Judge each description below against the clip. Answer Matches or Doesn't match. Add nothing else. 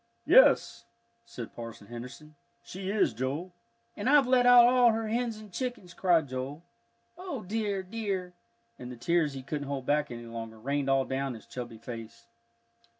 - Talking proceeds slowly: Doesn't match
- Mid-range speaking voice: Matches